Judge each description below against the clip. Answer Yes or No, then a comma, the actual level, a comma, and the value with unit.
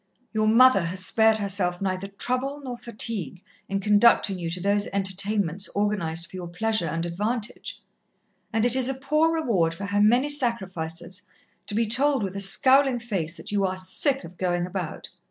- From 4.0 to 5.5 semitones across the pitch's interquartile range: Yes, average, 4.4 semitones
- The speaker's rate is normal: Yes, average, 175 wpm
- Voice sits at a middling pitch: No, high, 205 Hz